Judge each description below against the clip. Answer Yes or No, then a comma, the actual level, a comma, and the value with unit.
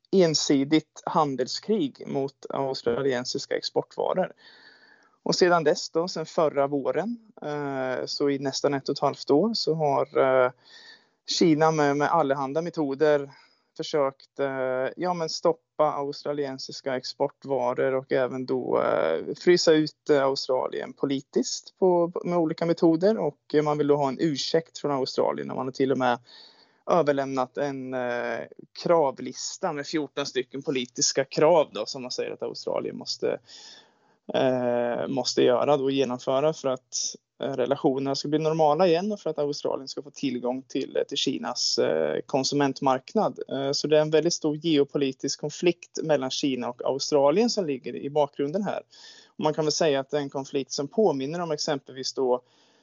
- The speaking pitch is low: No, medium, 145 Hz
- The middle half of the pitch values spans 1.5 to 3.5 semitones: Yes, average, 3.2 semitones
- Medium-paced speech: Yes, average, 145 wpm